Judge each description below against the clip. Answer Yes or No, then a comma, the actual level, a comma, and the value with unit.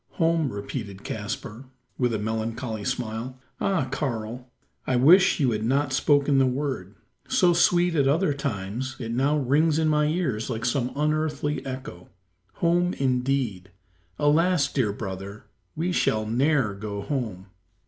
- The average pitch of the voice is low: Yes, low, 130 Hz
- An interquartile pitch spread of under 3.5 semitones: No, average, 5.2 semitones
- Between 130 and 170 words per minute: Yes, average, 140 wpm